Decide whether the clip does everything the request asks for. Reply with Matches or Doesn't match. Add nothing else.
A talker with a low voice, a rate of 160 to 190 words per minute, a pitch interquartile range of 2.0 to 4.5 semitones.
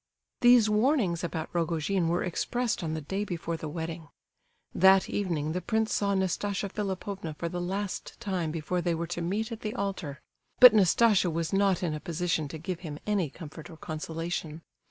Doesn't match